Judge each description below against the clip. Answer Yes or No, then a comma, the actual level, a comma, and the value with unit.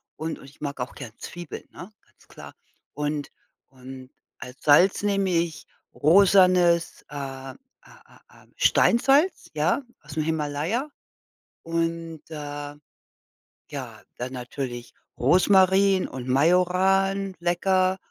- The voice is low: No, medium, 165 Hz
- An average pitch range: Yes, average, 4.6 semitones